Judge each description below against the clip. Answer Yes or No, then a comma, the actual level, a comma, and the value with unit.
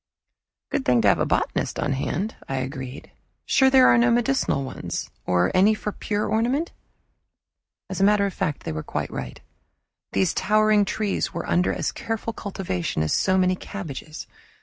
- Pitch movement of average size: No, wide, 8.3 semitones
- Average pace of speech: Yes, average, 170 wpm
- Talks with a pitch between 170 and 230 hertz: Yes, high, 190 Hz